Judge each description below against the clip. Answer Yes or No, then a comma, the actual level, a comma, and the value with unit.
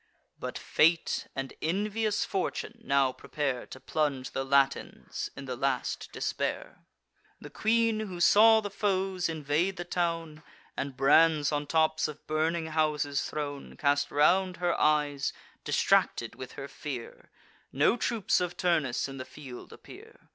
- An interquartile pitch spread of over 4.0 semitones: Yes, average, 4.6 semitones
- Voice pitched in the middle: Yes, medium, 155 Hz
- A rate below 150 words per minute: Yes, average, 140 wpm